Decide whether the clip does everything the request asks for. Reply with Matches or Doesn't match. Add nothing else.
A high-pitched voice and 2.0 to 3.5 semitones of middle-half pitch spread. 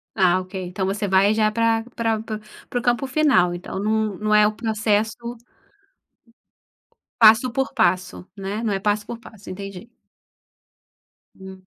Matches